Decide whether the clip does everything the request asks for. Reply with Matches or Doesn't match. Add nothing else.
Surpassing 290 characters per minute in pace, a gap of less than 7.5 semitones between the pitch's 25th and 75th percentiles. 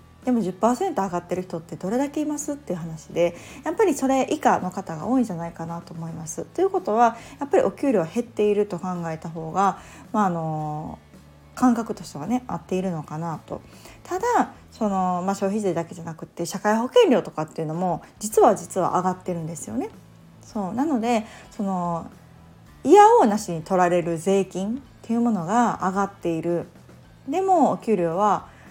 Matches